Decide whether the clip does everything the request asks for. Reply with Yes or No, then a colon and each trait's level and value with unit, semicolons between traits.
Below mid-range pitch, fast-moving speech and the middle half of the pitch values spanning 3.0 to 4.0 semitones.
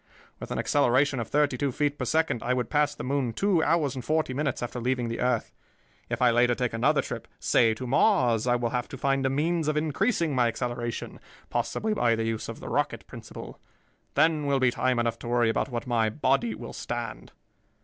Yes: low, 130 Hz; fast, 215 wpm; average, 3.7 semitones